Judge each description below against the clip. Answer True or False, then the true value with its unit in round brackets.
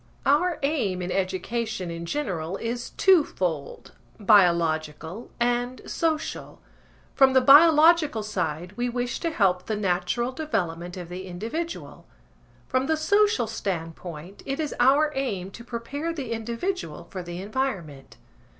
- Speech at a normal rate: False (130 wpm)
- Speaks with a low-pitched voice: False (230 Hz)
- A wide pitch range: True (7.5 semitones)